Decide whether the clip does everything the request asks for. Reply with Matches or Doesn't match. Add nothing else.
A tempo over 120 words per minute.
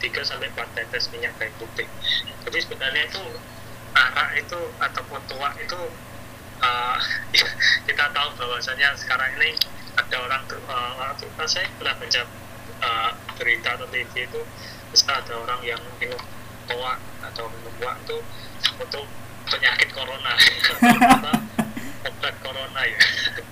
Matches